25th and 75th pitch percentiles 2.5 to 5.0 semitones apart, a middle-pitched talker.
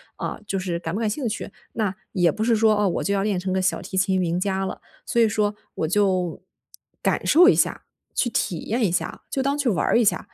No: average, 3.3 semitones; high, 200 Hz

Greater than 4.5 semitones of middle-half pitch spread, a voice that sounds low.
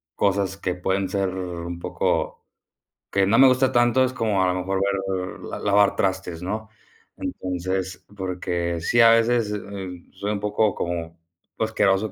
No: narrow, 2.5 semitones; very low, 95 Hz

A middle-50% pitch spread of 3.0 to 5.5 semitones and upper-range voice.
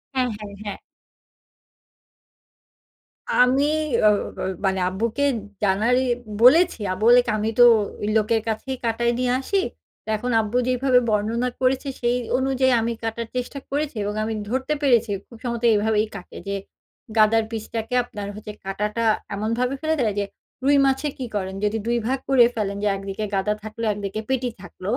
Yes: average, 3.3 semitones; high, 230 Hz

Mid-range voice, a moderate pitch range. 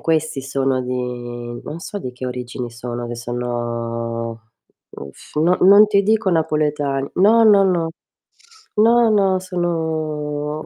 No: medium, 150 Hz; wide, 7.0 semitones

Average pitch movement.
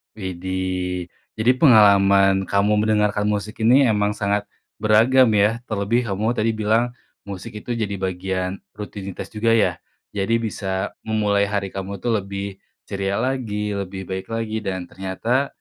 No: narrow, 2.1 semitones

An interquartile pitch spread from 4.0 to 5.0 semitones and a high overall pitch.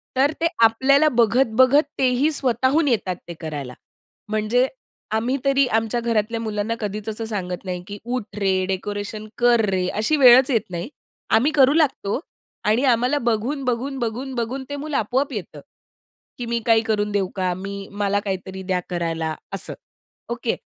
Yes: average, 4.5 semitones; high, 225 Hz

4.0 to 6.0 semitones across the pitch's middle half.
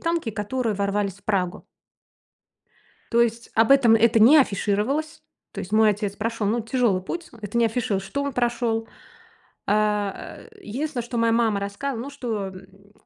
No: average, 3.1 semitones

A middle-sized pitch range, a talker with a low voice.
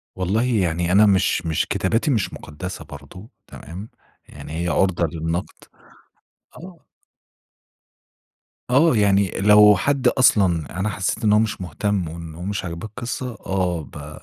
Yes: average, 4.1 semitones; very low, 95 Hz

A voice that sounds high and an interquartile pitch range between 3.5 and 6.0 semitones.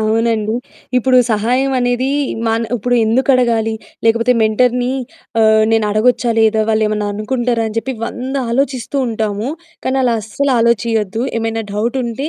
No: high, 230 Hz; narrow, 2.4 semitones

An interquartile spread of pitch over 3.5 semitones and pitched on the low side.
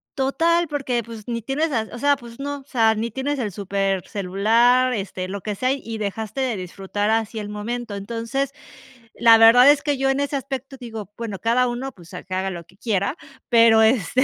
No: average, 4.5 semitones; high, 230 Hz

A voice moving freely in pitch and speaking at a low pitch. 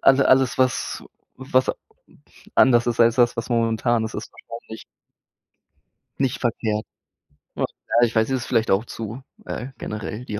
No: narrow, 2.4 semitones; low, 120 Hz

